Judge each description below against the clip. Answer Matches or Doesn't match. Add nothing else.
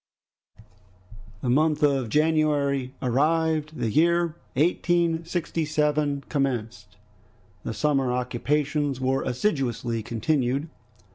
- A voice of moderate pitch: Matches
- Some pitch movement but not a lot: Matches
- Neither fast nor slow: Doesn't match